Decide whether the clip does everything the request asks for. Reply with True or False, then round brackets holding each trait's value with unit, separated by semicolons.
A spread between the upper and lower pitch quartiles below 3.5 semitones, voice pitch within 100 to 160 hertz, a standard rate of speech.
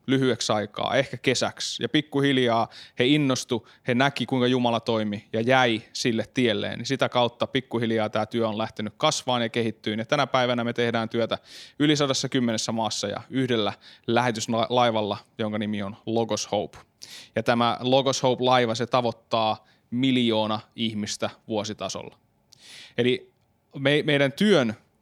True (2.5 semitones; 120 Hz; 135 wpm)